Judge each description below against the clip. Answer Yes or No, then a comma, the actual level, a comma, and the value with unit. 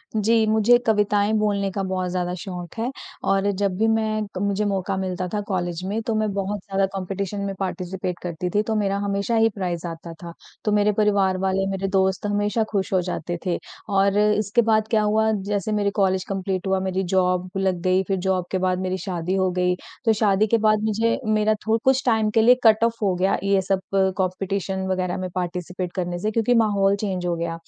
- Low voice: No, high, 195 Hz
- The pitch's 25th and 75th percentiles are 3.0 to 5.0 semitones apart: No, narrow, 2.4 semitones